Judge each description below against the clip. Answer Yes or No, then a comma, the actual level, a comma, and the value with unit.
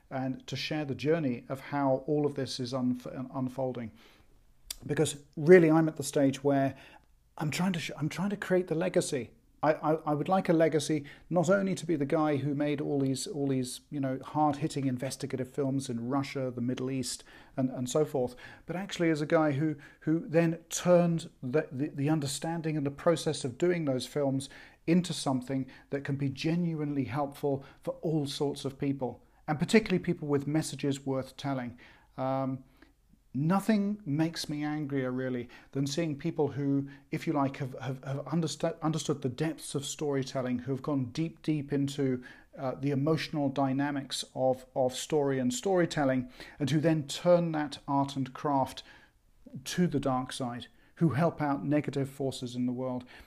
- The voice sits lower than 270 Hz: Yes, medium, 140 Hz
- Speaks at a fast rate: No, average, 180 wpm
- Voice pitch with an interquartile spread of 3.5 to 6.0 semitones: No, average, 2.9 semitones